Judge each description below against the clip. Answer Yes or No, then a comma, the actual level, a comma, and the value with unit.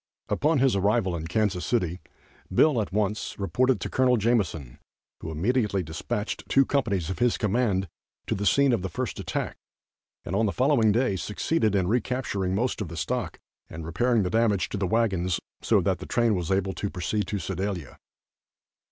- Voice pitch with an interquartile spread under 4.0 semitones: No, average, 4.4 semitones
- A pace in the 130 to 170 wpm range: No, average, 180 wpm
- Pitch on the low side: Yes, low, 105 Hz